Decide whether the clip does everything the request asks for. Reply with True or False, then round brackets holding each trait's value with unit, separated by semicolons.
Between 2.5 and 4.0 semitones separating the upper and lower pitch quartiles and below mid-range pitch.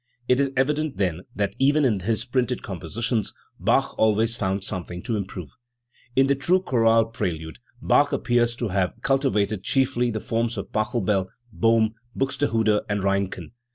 False (4.4 semitones; 115 Hz)